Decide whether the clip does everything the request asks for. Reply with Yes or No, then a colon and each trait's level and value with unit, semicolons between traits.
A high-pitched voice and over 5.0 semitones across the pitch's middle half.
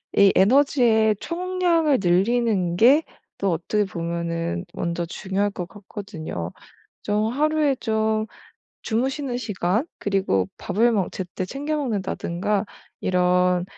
Yes: high, 205 Hz; wide, 5.4 semitones